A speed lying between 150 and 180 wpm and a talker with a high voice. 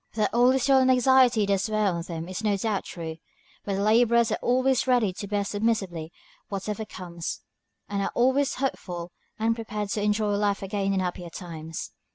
No: average, 190 wpm; high, 205 Hz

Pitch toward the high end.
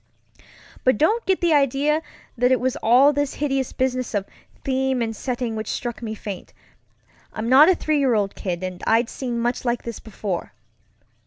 Yes: very high, 250 Hz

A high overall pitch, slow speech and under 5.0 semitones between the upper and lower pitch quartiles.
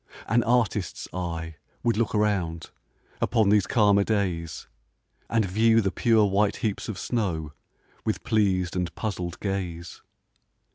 No: low, 100 Hz; slow, 130 wpm; average, 3.8 semitones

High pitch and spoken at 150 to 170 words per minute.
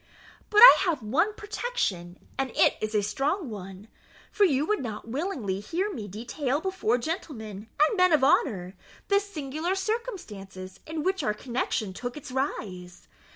Yes: very high, 265 Hz; average, 155 wpm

